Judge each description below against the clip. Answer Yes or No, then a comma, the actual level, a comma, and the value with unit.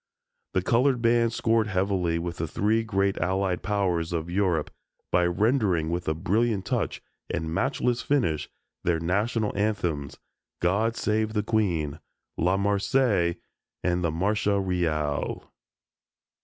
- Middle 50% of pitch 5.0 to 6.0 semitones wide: No, average, 4.1 semitones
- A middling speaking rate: No, slow, 130 wpm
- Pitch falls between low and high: No, very low, 95 Hz